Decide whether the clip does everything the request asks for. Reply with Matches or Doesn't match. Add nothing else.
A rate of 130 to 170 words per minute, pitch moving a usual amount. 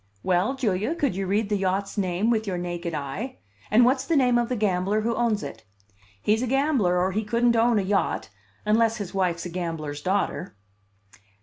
Doesn't match